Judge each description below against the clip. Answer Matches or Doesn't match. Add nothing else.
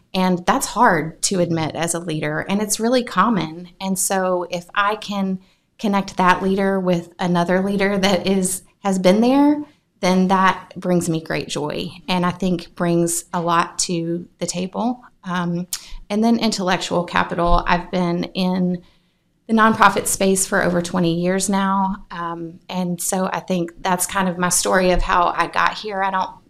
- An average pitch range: Doesn't match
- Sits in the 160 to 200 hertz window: Matches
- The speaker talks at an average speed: Matches